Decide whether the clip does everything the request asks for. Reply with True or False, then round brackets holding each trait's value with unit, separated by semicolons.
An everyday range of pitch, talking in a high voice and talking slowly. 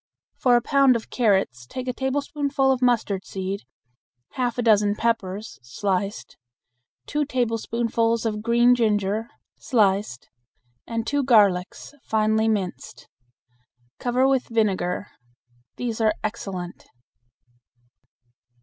True (3.6 semitones; 225 Hz; 105 wpm)